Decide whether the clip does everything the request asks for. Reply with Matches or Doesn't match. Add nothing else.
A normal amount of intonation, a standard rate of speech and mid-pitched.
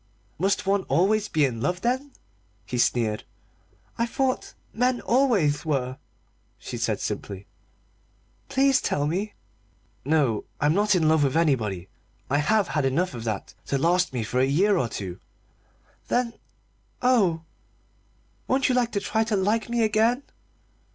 Doesn't match